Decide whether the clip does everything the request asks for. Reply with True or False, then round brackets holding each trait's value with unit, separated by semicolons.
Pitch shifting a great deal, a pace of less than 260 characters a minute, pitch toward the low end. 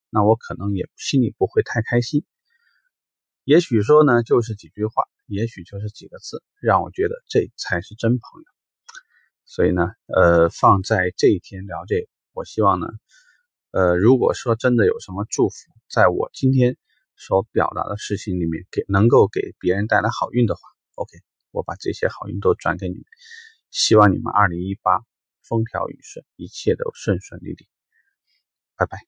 True (9.0 semitones; 250 characters per minute; 115 Hz)